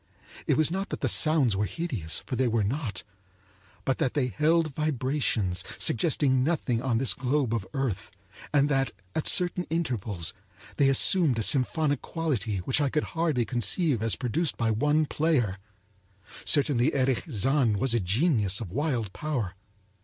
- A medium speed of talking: Yes, average, 160 wpm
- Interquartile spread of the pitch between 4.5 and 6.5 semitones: Yes, average, 5.1 semitones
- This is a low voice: Yes, low, 130 Hz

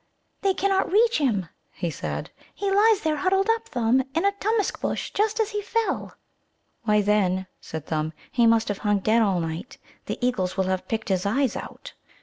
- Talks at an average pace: Yes, average, 190 wpm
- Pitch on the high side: Yes, high, 245 Hz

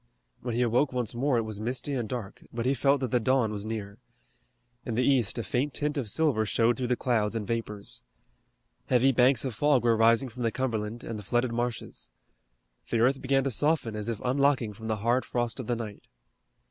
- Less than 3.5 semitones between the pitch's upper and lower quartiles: Yes, average, 2.7 semitones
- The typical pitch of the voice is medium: No, low, 120 Hz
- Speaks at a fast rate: Yes, fast, 215 wpm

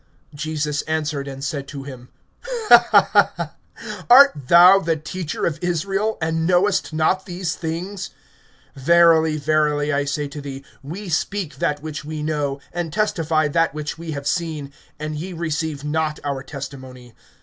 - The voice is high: No, medium, 155 Hz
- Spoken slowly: No, average, 145 wpm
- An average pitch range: Yes, average, 3.0 semitones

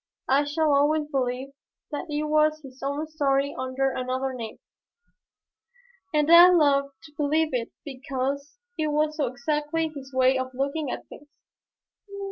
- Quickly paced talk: No, average, 145 wpm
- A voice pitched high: Yes, very high, 280 Hz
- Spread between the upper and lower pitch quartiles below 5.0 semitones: Yes, narrow, 2.5 semitones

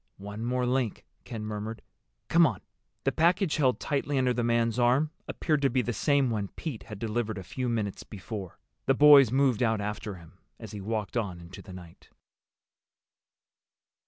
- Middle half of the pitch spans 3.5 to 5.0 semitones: Yes, average, 4.1 semitones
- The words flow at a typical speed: Yes, average, 175 wpm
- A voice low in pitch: Yes, low, 115 Hz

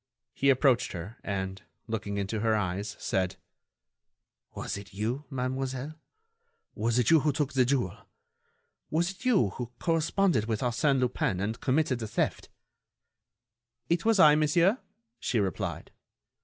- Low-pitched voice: Yes, low, 125 Hz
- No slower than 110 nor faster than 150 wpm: Yes, average, 140 wpm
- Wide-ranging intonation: Yes, wide, 6.3 semitones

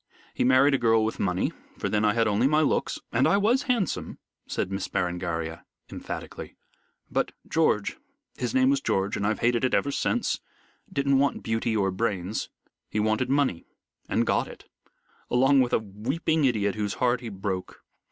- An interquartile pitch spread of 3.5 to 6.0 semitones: Yes, wide, 5.4 semitones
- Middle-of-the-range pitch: No, low, 115 Hz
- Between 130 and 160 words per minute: No, average, 175 wpm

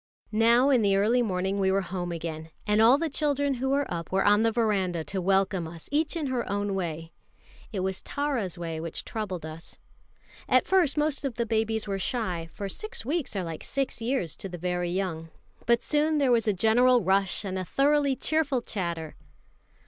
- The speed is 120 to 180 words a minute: No, average, 200 wpm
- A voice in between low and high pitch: No, high, 210 Hz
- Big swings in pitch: Yes, wide, 6.3 semitones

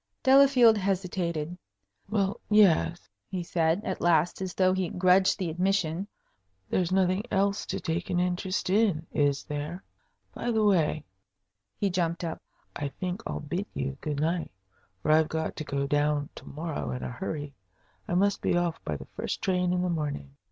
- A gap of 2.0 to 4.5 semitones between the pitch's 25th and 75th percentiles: Yes, average, 3.5 semitones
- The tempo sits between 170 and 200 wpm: Yes, average, 175 wpm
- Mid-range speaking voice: Yes, medium, 175 Hz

